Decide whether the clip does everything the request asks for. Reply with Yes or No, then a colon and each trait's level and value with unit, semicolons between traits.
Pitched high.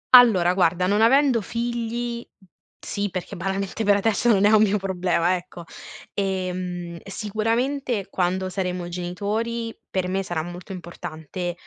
Yes: high, 195 Hz